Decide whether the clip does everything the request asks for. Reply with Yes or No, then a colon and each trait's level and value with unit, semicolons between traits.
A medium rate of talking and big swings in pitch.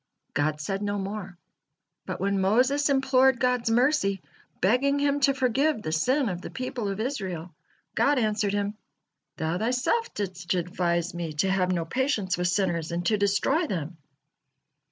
Yes: average, 155 wpm; wide, 6.3 semitones